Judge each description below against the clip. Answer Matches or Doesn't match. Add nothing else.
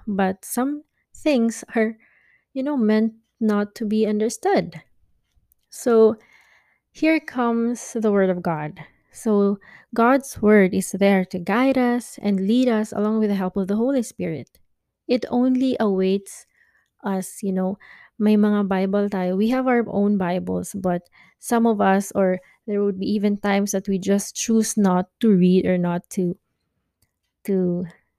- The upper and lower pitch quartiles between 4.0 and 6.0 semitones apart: Doesn't match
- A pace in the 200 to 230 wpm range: Doesn't match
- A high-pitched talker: Matches